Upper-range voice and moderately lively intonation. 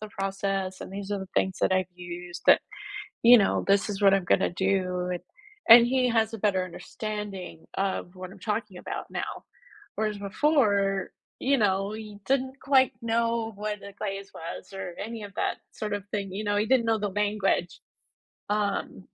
No: high, 200 Hz; narrow, 2.2 semitones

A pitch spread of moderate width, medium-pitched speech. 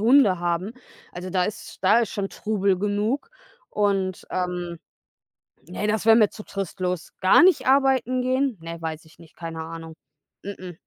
No: average, 4.0 semitones; high, 195 Hz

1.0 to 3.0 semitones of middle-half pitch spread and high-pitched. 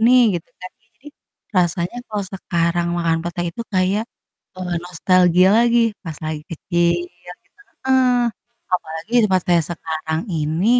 No: narrow, 2.4 semitones; medium, 175 Hz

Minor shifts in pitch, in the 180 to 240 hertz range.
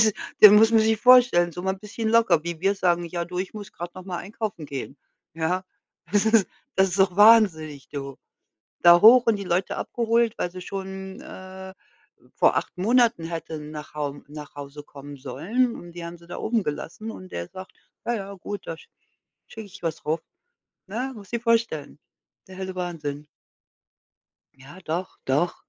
No: average, 4.8 semitones; medium, 185 Hz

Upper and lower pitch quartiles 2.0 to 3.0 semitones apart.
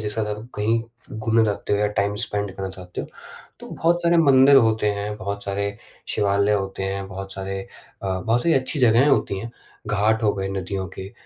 Yes: narrow, 2.6 semitones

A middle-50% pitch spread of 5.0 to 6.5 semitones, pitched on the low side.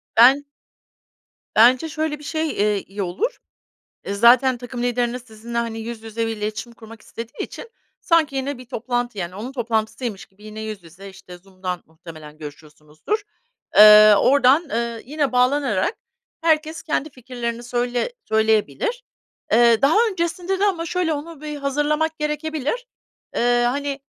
No: wide, 5.5 semitones; high, 245 Hz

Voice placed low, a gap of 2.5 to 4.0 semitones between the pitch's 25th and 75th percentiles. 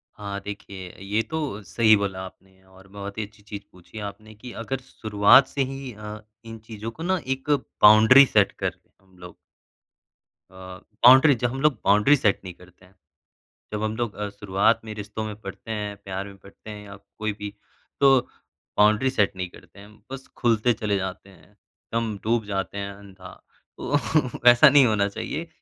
Yes: low, 105 Hz; average, 3.1 semitones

